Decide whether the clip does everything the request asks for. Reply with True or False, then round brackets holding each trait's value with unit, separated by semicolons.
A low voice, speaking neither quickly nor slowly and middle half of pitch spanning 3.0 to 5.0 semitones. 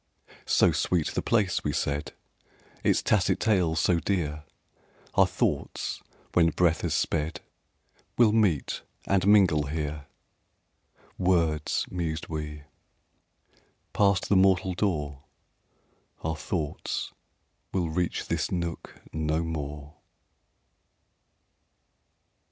False (80 Hz; 100 wpm; 3.4 semitones)